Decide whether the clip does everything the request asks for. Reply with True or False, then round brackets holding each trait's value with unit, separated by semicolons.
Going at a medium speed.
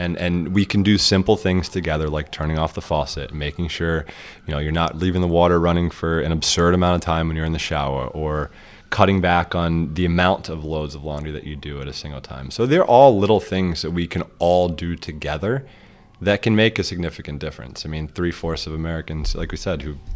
False (230 wpm)